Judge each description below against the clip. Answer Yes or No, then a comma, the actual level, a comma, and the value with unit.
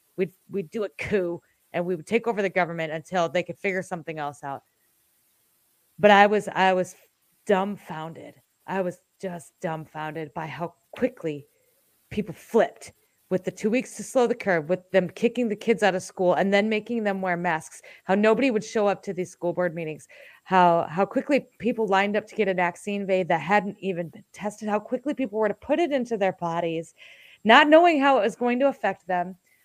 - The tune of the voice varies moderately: Yes, average, 3.9 semitones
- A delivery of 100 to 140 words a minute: No, average, 200 wpm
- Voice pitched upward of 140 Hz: Yes, high, 190 Hz